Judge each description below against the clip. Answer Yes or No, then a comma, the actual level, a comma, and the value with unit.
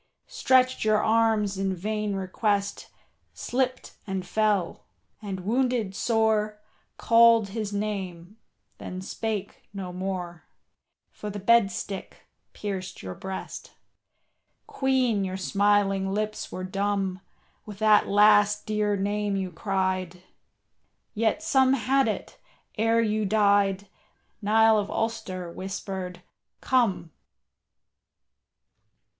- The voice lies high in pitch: Yes, high, 205 Hz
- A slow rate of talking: Yes, slow, 105 wpm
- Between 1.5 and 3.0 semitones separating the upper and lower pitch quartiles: Yes, narrow, 2.4 semitones